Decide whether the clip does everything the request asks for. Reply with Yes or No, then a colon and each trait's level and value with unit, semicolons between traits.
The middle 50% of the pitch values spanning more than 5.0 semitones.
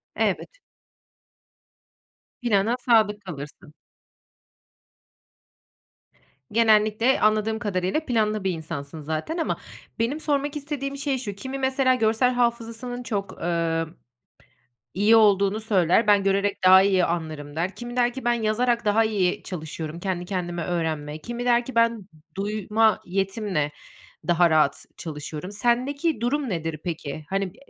Yes: wide, 5.4 semitones